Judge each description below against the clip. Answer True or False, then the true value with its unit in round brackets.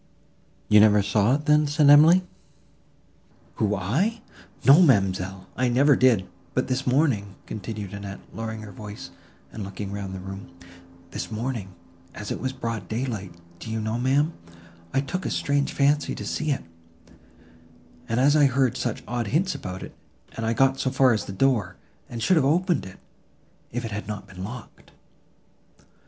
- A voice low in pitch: True (115 Hz)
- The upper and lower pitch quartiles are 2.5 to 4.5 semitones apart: False (5.3 semitones)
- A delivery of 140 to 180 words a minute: True (170 wpm)